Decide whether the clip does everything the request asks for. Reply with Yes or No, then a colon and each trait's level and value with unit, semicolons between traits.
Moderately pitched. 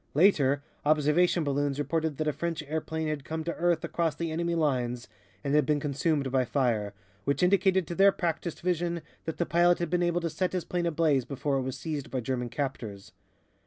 Yes: medium, 155 Hz